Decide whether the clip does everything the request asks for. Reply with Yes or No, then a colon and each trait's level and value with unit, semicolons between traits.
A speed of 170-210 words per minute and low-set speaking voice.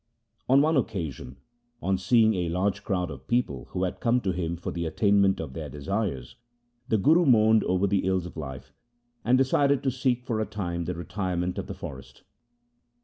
Yes: average, 190 wpm; very low, 95 Hz